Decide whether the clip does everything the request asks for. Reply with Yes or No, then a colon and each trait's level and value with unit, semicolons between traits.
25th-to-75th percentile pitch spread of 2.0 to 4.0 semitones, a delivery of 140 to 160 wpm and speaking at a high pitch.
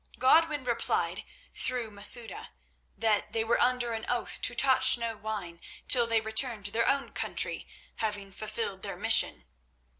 Yes: average, 2.7 semitones; average, 150 wpm; high, 230 Hz